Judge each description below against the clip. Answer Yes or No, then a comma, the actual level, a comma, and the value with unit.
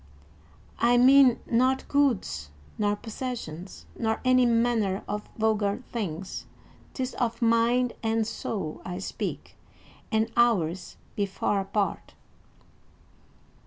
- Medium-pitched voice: No, high, 225 Hz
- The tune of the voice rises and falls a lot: No, average, 3.5 semitones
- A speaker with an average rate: No, slow, 105 wpm